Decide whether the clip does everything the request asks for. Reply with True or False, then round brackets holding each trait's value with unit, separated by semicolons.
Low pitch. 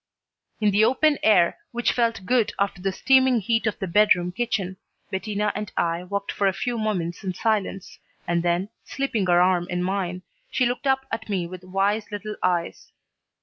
False (200 Hz)